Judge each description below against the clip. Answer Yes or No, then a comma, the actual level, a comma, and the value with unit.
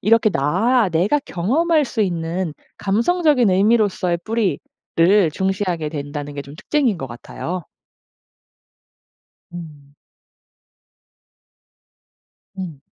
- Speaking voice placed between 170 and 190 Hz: Yes, medium, 185 Hz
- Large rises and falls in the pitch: Yes, wide, 5.8 semitones